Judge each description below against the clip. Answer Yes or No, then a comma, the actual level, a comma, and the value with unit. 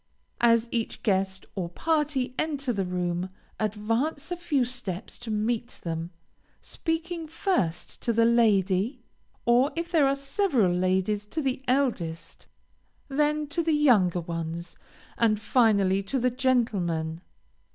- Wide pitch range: Yes, wide, 6.7 semitones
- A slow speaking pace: Yes, slow, 130 wpm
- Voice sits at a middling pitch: No, high, 230 Hz